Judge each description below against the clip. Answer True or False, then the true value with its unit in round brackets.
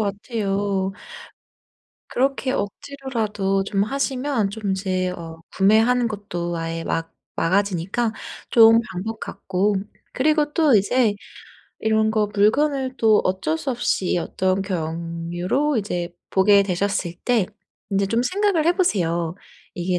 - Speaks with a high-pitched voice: True (205 Hz)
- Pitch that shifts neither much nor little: True (4.7 semitones)